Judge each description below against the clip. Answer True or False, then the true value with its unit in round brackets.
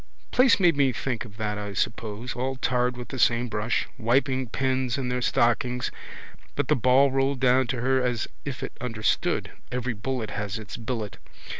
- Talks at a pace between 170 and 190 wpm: True (180 wpm)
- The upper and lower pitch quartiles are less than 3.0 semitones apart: True (2.5 semitones)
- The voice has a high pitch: False (125 Hz)